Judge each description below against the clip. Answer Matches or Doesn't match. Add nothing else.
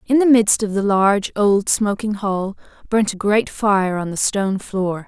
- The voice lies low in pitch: Doesn't match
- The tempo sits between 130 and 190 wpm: Doesn't match